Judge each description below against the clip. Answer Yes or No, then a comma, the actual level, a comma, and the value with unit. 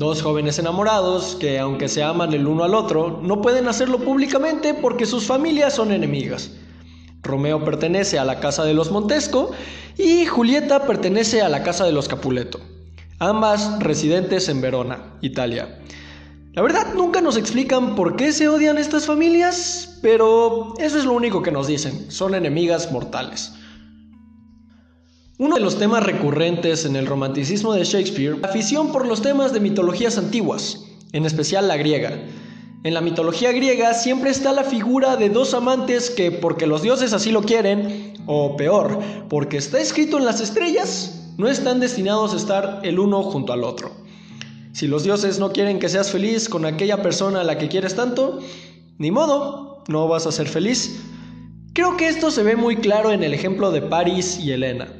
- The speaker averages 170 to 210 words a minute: Yes, average, 175 wpm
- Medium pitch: No, high, 195 Hz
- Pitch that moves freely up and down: Yes, wide, 7.9 semitones